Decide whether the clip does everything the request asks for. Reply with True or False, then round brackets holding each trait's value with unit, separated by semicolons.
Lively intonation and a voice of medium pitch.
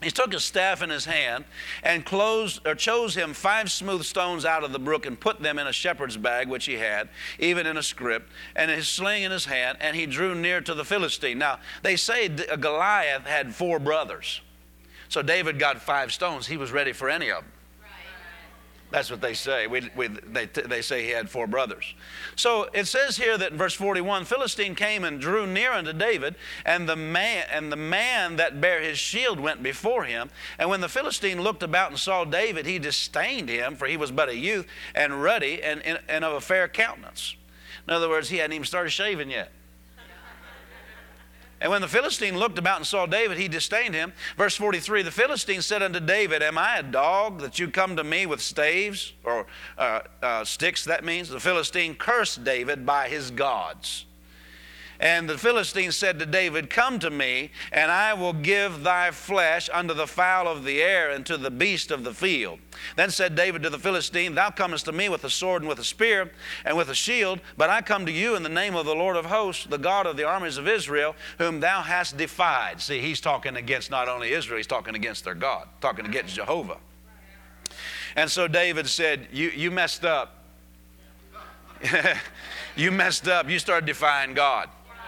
False (4.6 semitones; 170 Hz)